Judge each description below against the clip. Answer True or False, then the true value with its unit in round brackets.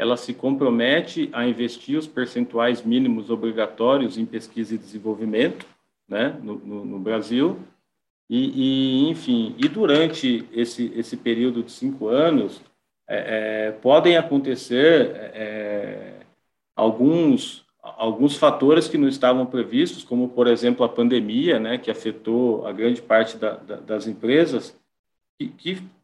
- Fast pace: False (135 wpm)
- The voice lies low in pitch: True (120 Hz)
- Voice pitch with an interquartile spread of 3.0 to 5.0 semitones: True (3.8 semitones)